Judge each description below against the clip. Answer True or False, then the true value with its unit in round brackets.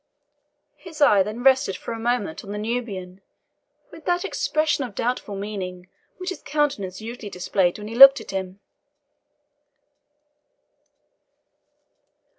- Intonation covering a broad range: True (5.9 semitones)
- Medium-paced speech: False (125 wpm)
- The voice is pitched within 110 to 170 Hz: False (220 Hz)